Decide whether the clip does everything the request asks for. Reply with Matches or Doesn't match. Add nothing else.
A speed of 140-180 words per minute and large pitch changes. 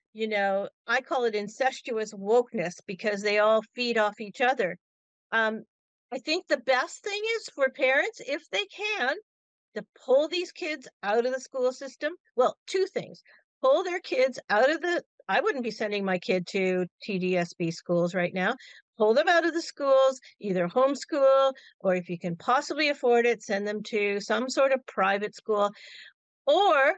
Matches